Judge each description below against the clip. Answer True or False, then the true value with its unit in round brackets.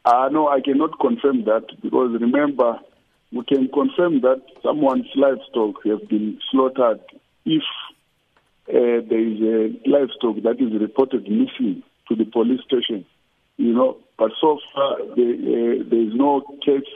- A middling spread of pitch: True (4.0 semitones)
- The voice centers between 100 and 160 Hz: True (135 Hz)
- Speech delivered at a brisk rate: False (150 wpm)